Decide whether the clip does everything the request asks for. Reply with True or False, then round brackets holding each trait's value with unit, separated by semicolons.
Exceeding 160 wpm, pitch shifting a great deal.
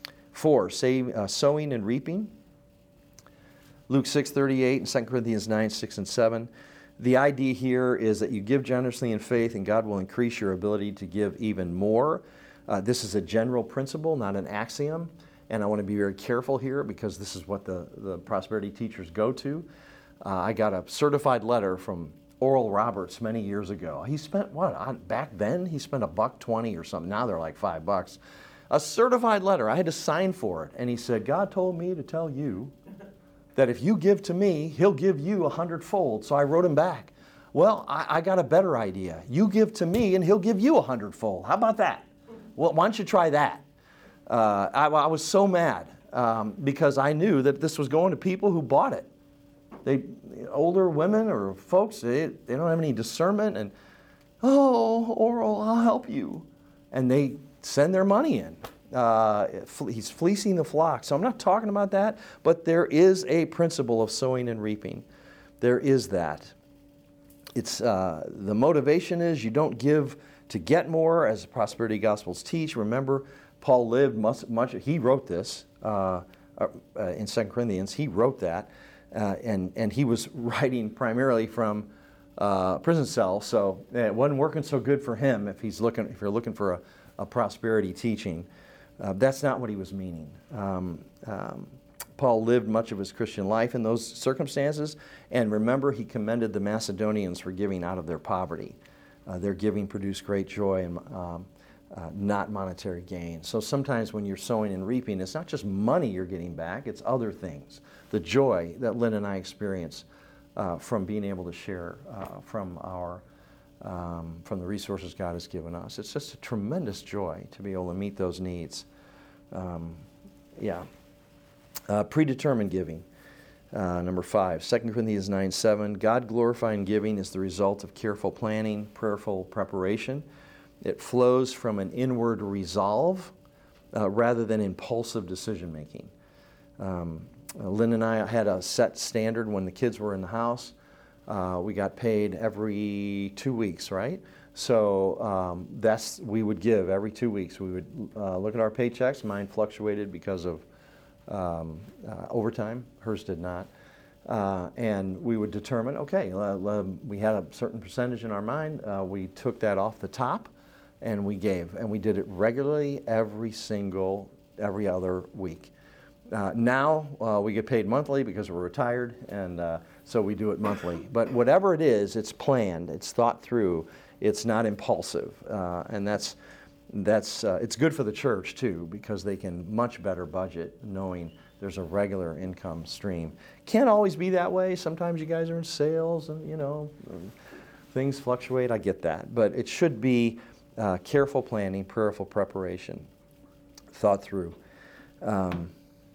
True (175 wpm; 6.3 semitones)